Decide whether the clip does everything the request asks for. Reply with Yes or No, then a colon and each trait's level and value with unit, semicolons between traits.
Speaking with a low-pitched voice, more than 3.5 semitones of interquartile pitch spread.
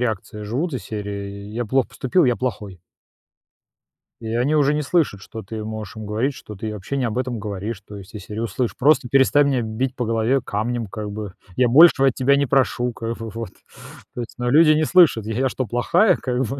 Yes: low, 120 Hz; average, 3.9 semitones